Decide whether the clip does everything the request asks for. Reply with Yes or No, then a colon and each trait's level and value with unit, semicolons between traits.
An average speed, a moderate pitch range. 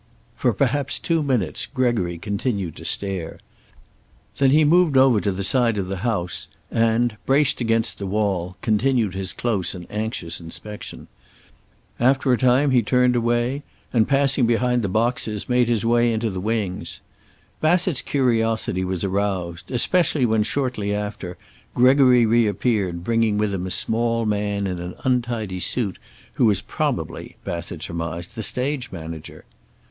Yes: average, 150 wpm; average, 4.4 semitones